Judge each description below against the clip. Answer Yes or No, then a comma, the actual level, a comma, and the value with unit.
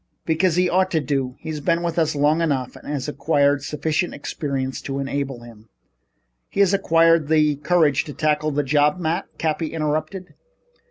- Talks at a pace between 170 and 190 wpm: Yes, average, 175 wpm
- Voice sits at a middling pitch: Yes, medium, 150 Hz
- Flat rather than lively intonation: No, average, 3.0 semitones